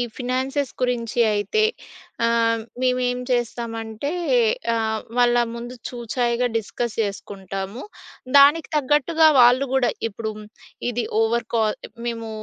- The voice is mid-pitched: No, high, 240 Hz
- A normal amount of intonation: No, narrow, 2.1 semitones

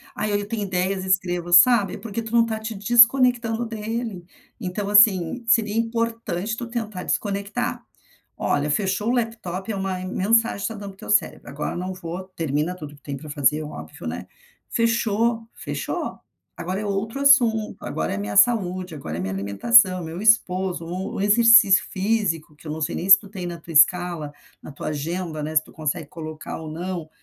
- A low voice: No, high, 190 Hz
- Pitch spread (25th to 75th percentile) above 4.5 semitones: Yes, average, 5.1 semitones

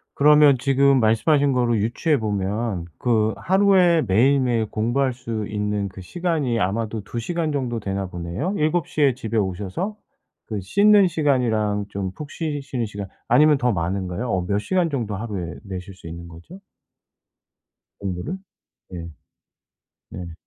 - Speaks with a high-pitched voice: No, low, 115 Hz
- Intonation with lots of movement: Yes, wide, 6.6 semitones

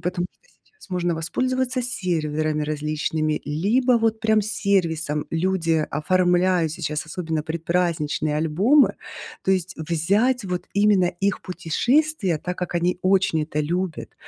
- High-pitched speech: No, medium, 180 Hz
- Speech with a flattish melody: No, average, 4.2 semitones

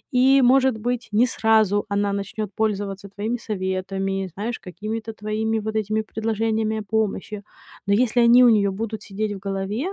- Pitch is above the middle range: Yes, high, 215 Hz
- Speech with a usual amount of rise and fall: No, narrow, 1.9 semitones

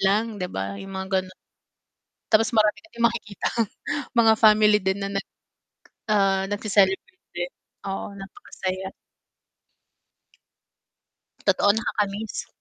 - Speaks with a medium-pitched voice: No, high, 200 Hz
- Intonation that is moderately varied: No, narrow, 2.1 semitones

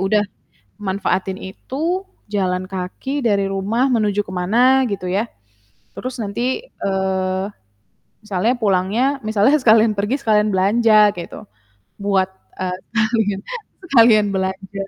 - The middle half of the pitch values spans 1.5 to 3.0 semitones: Yes, narrow, 2.6 semitones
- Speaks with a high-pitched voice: Yes, high, 200 Hz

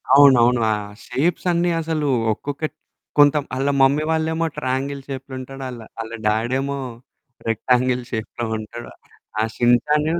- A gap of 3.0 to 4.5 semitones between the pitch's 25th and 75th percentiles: Yes, average, 3.4 semitones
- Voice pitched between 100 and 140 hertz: Yes, low, 135 Hz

